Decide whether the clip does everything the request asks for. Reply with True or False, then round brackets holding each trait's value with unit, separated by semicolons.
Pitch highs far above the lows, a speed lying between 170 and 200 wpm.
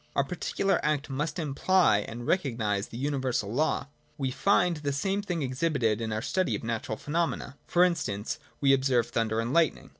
True (6.4 semitones; 180 wpm)